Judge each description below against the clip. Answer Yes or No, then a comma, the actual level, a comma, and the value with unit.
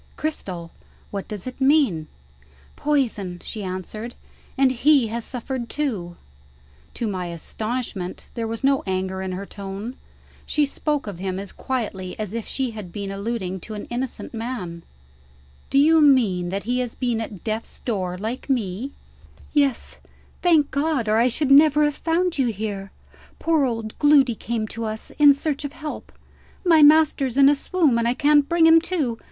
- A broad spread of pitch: Yes, wide, 6.0 semitones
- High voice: Yes, high, 235 Hz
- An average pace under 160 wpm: No, average, 170 wpm